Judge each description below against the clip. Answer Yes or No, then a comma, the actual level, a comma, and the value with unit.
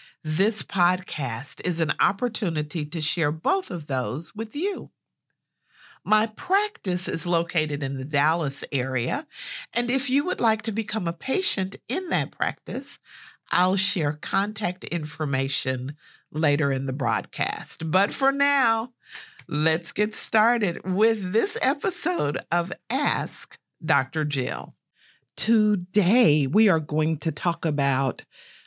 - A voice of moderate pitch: Yes, medium, 175 Hz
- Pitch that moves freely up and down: Yes, wide, 6.4 semitones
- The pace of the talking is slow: Yes, slow, 125 wpm